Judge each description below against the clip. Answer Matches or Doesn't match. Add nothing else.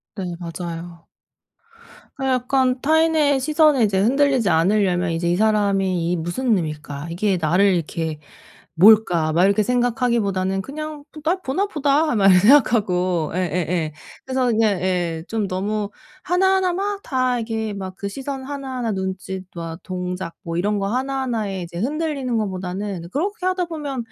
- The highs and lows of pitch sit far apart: Matches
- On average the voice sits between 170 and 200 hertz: Doesn't match